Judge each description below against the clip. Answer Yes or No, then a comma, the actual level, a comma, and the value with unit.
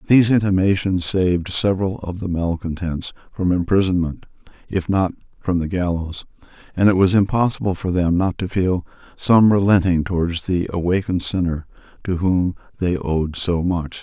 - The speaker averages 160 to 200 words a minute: No, average, 150 wpm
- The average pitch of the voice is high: No, very low, 90 Hz